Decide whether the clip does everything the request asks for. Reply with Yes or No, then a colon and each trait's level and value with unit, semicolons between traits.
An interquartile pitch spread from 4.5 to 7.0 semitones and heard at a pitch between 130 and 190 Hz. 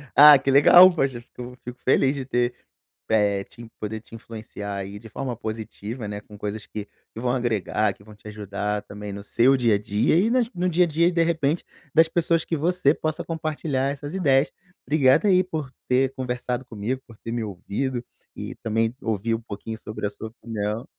No: average, 5.2 semitones; low, 120 Hz